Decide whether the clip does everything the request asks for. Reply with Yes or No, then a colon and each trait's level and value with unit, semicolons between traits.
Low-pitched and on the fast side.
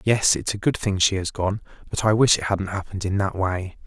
Yes: low, 100 Hz; fast, 265 wpm